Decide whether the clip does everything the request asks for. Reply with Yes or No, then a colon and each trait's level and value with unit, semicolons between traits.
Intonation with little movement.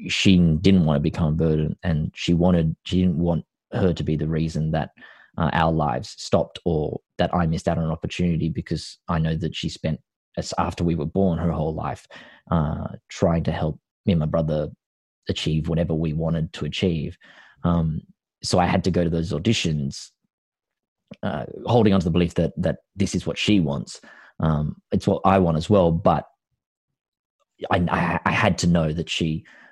Yes: narrow, 1.8 semitones